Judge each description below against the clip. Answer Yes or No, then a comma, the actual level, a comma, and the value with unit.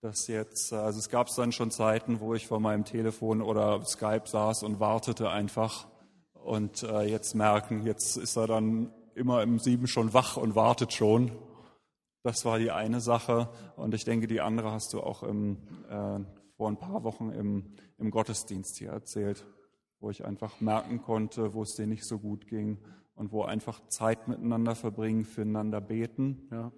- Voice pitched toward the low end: Yes, low, 110 Hz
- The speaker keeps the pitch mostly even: Yes, narrow, 1.2 semitones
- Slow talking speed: No, average, 175 wpm